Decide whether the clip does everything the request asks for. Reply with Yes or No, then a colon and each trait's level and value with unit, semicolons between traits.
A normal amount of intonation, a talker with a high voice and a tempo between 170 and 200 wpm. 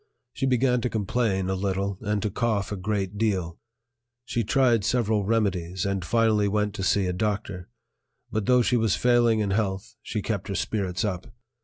No: average, 3.0 semitones; low, 105 Hz; average, 180 wpm